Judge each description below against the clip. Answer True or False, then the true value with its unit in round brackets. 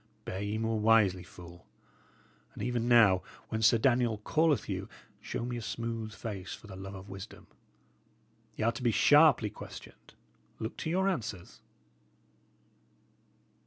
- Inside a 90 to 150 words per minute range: True (145 wpm)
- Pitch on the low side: True (110 Hz)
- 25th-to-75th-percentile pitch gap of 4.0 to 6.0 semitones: False (3.4 semitones)